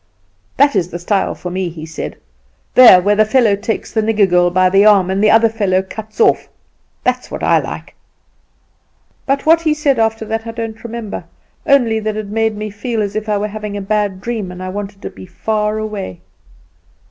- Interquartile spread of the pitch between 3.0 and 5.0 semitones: No, narrow, 2.5 semitones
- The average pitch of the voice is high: Yes, high, 215 Hz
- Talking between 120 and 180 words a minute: No, fast, 205 wpm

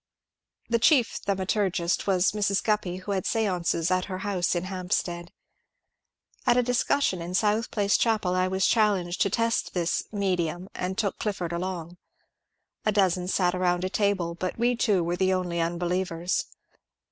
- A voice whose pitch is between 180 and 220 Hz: Yes, medium, 185 Hz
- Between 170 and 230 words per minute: No, average, 160 wpm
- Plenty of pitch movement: No, average, 2.7 semitones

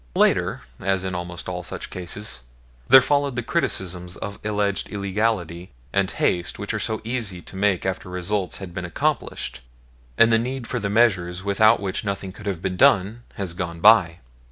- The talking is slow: No, average, 180 wpm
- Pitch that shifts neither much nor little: Yes, average, 3.3 semitones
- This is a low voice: Yes, very low, 95 Hz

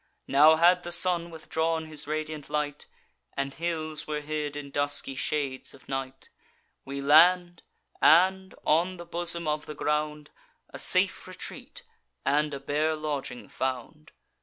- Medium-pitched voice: Yes, medium, 150 Hz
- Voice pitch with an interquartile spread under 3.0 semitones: Yes, narrow, 2.5 semitones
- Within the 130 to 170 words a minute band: Yes, average, 140 wpm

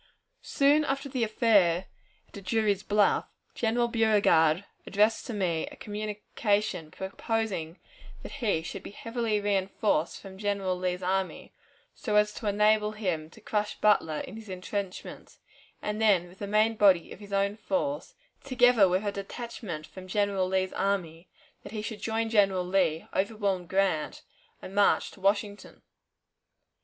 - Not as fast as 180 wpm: Yes, average, 150 wpm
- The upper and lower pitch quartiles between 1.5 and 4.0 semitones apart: Yes, average, 2.7 semitones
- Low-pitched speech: No, high, 205 Hz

